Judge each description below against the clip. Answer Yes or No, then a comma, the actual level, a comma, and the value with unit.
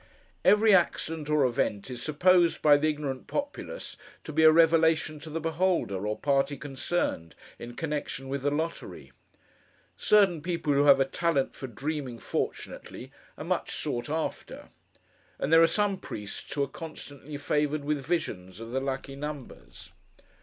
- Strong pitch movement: No, average, 3.3 semitones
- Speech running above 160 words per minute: No, average, 155 wpm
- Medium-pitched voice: Yes, medium, 150 Hz